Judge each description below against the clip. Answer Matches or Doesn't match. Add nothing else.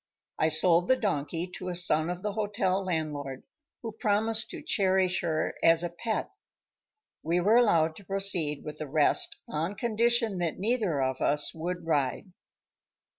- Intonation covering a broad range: Doesn't match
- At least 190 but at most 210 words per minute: Doesn't match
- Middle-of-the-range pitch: Matches